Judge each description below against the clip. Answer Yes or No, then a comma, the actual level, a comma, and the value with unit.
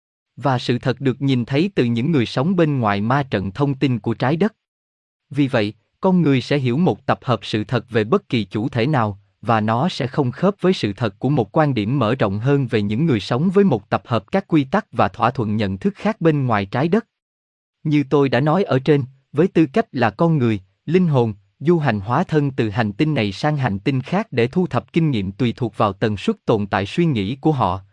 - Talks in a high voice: No, low, 125 Hz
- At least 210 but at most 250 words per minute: Yes, average, 245 wpm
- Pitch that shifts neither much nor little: No, wide, 5.8 semitones